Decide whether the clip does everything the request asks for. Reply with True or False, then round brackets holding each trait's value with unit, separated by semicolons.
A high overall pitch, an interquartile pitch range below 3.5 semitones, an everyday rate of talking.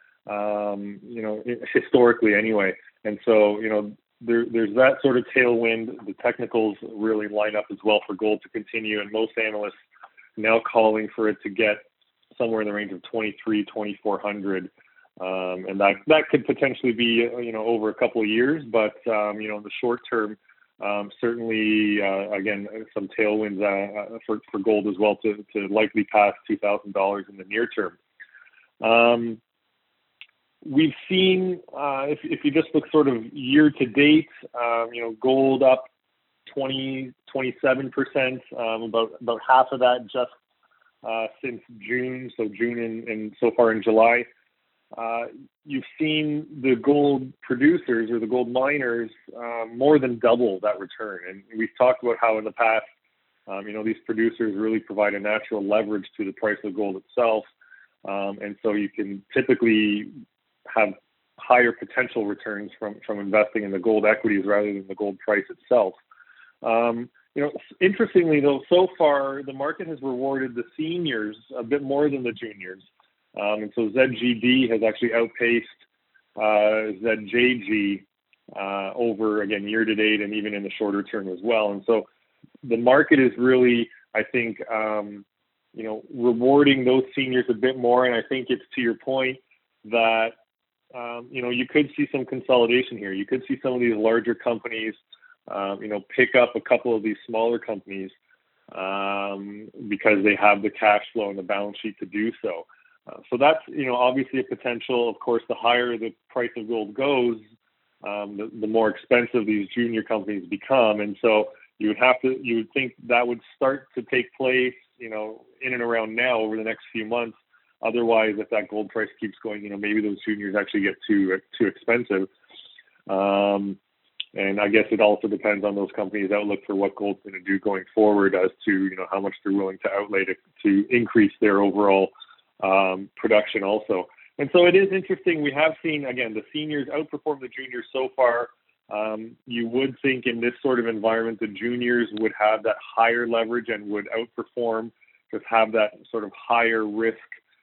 False (115 Hz; 3.1 semitones; 180 wpm)